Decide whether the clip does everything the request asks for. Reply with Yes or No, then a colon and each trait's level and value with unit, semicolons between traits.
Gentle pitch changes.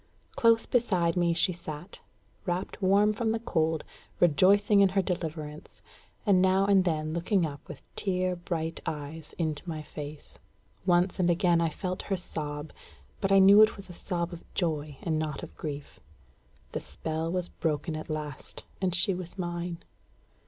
No: average, 3.2 semitones